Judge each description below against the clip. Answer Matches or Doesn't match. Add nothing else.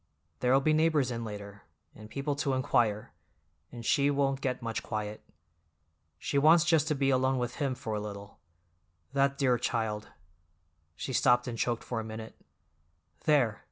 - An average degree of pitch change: Matches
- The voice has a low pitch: Matches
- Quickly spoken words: Doesn't match